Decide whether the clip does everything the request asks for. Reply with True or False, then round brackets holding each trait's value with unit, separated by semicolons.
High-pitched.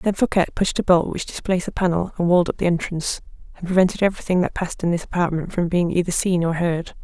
False (175 Hz)